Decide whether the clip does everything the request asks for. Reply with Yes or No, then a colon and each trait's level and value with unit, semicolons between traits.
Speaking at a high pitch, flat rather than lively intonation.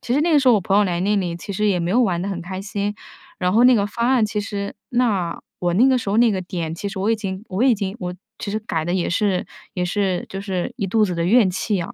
No: high, 200 Hz; average, 3.3 semitones